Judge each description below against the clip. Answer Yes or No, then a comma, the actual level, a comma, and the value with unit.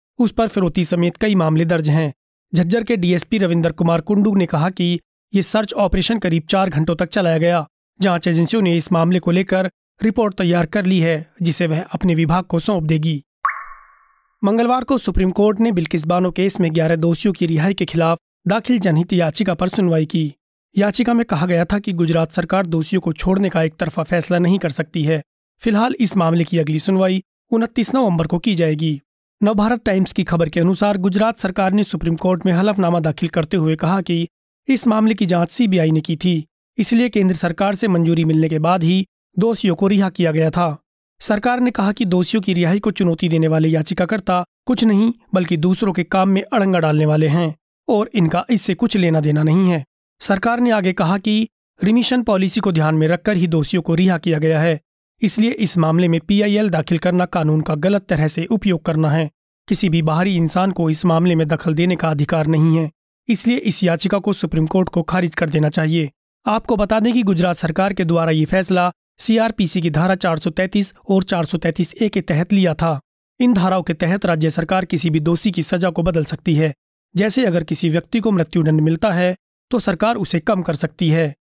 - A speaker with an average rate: No, fast, 205 wpm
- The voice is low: No, medium, 180 Hz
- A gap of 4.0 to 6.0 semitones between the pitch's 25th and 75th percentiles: No, average, 3.4 semitones